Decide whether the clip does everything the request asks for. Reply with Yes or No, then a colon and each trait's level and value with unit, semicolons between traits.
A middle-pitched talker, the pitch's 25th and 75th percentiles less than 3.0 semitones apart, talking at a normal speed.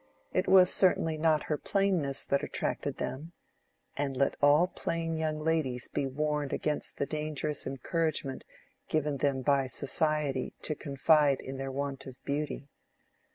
Yes: medium, 150 Hz; narrow, 2.4 semitones; average, 145 wpm